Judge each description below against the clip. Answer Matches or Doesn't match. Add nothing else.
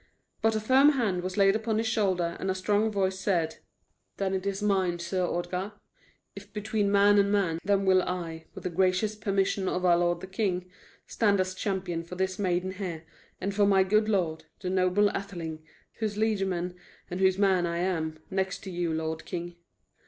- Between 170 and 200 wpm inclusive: Matches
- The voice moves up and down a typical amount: Doesn't match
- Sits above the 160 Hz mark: Matches